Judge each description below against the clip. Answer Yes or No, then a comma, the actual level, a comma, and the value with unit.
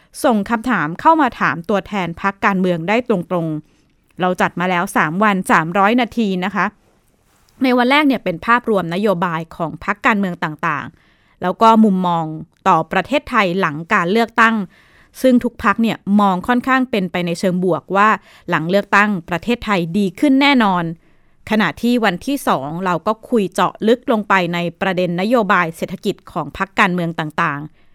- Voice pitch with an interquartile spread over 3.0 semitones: Yes, average, 4.4 semitones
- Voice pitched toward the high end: Yes, high, 195 Hz